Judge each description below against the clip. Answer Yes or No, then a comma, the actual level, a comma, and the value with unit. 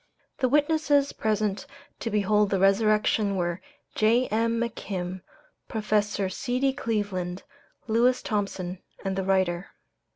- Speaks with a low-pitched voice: No, high, 210 Hz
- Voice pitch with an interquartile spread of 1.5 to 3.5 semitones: Yes, average, 3.2 semitones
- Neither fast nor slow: No, slow, 105 wpm